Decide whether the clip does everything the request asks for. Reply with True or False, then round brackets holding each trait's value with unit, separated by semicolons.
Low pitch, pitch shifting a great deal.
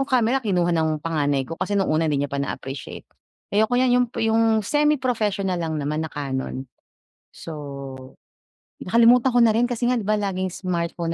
False (185 Hz; 7.0 semitones)